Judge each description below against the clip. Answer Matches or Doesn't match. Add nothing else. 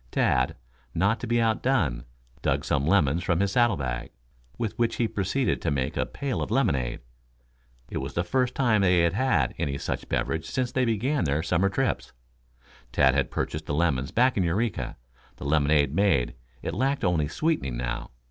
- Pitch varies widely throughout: Matches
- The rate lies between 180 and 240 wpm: Matches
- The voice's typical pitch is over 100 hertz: Doesn't match